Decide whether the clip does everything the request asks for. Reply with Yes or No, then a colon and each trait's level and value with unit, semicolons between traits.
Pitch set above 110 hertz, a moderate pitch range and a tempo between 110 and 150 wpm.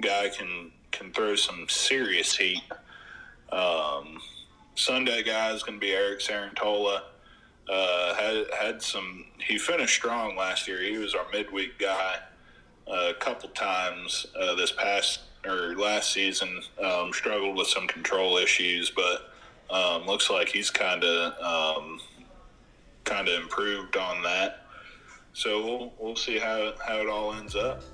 No: low, 100 Hz; average, 3.0 semitones; average, 145 wpm